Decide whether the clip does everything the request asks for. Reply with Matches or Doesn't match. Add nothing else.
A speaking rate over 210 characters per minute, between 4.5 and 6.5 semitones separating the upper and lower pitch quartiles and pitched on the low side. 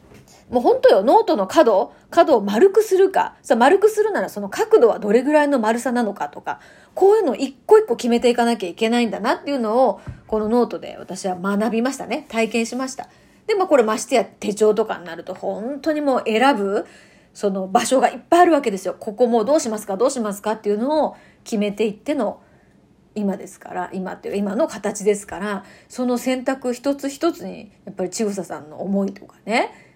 Doesn't match